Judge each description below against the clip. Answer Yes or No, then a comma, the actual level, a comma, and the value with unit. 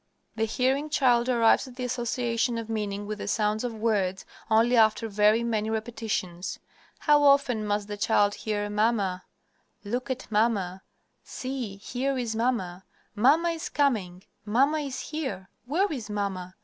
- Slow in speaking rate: No, average, 150 wpm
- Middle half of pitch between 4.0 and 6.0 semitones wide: No, average, 3.5 semitones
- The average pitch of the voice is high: Yes, high, 225 Hz